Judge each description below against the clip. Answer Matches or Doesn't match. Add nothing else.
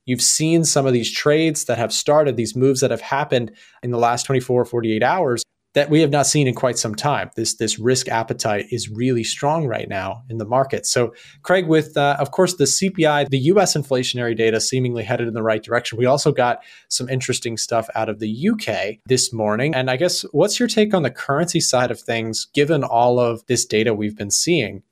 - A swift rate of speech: Matches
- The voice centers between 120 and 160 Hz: Matches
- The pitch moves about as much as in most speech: Matches